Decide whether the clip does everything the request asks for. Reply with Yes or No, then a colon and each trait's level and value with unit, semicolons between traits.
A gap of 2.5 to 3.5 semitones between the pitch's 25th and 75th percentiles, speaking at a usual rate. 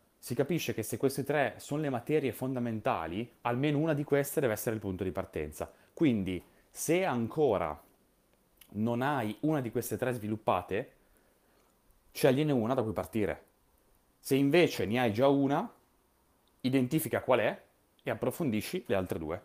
No: average, 4.5 semitones; average, 150 wpm